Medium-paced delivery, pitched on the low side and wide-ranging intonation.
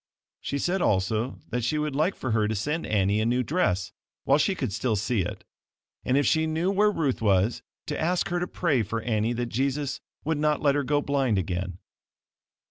No: fast, 210 wpm; low, 130 Hz; wide, 5.8 semitones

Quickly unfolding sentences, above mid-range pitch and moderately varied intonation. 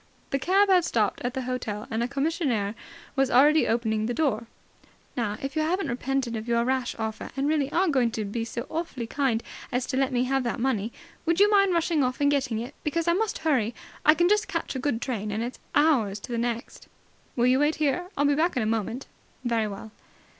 Yes: fast, 225 wpm; very high, 255 Hz; average, 4.7 semitones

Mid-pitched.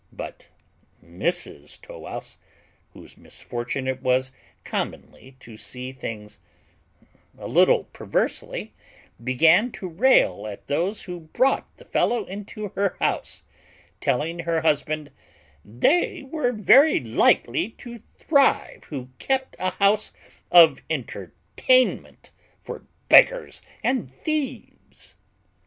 Yes: medium, 165 Hz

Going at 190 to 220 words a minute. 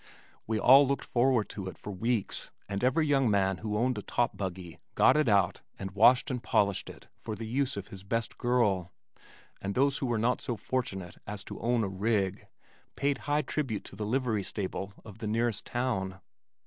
Yes: average, 200 wpm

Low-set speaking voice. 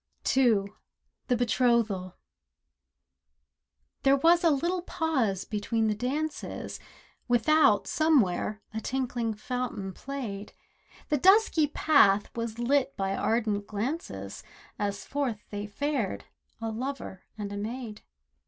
No: high, 235 Hz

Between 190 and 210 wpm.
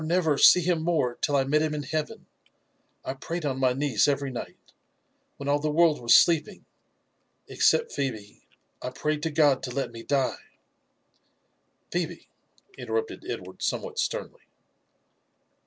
No: average, 155 wpm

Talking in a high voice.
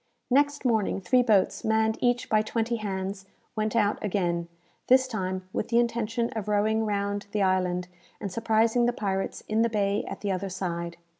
Yes: high, 215 Hz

